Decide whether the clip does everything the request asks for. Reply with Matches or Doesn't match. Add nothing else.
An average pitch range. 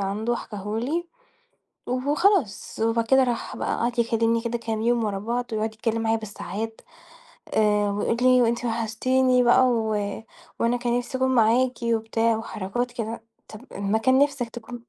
Doesn't match